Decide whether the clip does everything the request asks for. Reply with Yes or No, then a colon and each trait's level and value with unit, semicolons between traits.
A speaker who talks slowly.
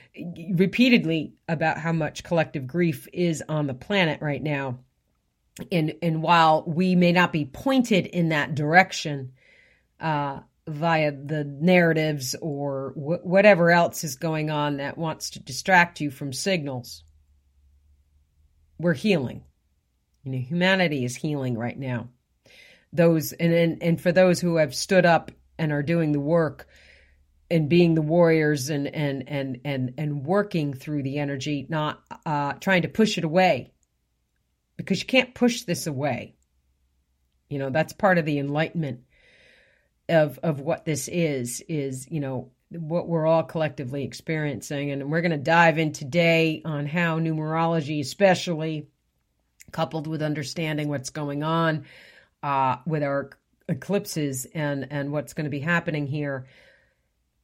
No: average, 145 wpm